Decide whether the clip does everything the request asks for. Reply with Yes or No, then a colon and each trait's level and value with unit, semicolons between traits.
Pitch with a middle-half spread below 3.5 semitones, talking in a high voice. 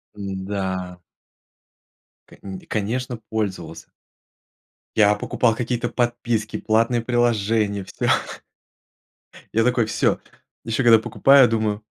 No: average, 2.9 semitones; low, 110 Hz